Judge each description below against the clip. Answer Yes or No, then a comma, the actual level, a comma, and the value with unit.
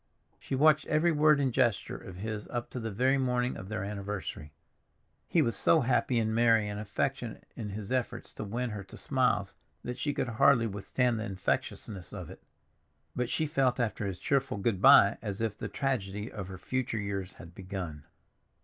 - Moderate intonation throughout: Yes, average, 4.4 semitones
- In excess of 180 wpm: Yes, average, 190 wpm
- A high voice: No, low, 115 Hz